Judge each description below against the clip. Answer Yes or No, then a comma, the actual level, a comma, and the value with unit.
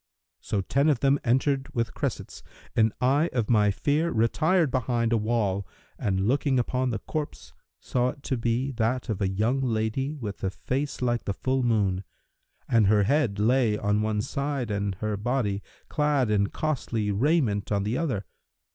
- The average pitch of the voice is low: Yes, low, 120 Hz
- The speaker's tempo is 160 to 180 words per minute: Yes, average, 175 wpm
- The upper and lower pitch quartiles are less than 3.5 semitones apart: No, average, 4.4 semitones